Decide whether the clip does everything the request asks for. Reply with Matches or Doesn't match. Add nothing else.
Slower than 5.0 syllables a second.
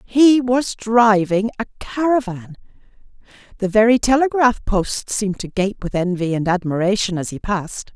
Matches